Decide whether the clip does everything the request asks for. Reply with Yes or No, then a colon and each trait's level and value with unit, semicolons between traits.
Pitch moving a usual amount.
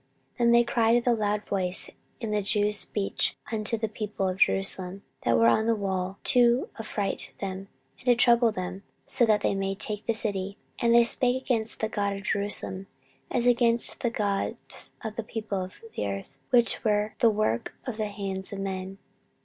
Yes: average, 3.0 semitones